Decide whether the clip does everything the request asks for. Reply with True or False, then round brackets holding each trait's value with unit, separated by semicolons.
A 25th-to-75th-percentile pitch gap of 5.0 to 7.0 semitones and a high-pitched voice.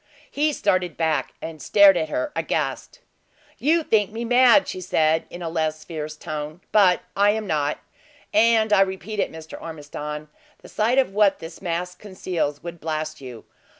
False (5.3 semitones; 175 Hz)